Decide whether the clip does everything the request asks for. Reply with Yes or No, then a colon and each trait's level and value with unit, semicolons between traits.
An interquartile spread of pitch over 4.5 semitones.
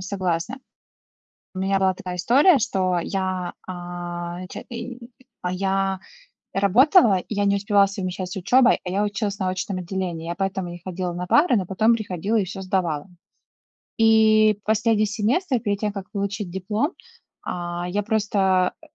No: average, 2.9 semitones